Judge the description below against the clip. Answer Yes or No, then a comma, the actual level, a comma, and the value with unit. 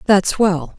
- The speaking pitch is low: No, medium, 185 Hz